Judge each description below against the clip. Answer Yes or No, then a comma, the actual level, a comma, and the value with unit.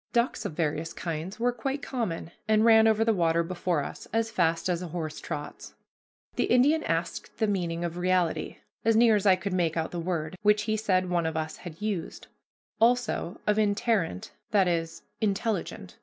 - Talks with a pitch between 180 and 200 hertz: Yes, medium, 185 Hz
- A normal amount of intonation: Yes, average, 4.8 semitones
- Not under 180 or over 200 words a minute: Yes, average, 185 wpm